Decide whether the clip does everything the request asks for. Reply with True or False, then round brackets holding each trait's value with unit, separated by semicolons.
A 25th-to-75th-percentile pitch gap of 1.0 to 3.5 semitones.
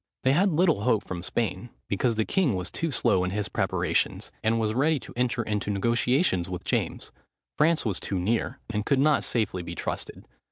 False (5.5 semitones)